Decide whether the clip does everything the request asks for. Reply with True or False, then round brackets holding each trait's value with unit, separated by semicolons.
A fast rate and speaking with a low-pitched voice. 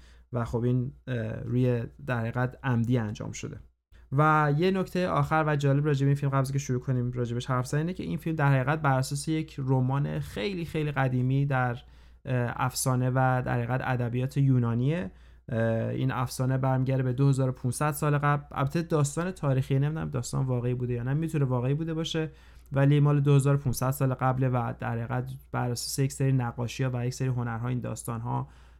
True (175 wpm; 130 Hz)